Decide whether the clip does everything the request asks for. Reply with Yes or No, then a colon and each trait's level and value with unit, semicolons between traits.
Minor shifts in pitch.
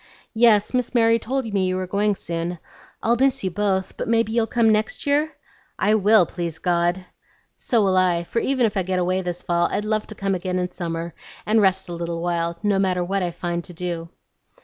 No: average, 3.8 semitones